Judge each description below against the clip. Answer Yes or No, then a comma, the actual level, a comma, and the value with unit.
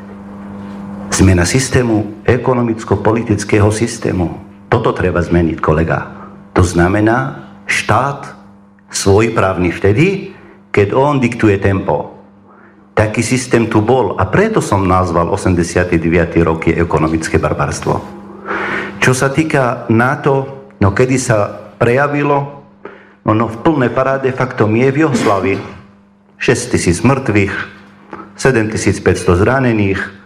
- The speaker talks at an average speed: No, slow, 105 wpm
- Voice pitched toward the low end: Yes, low, 105 Hz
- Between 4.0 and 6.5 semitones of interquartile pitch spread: Yes, average, 4.4 semitones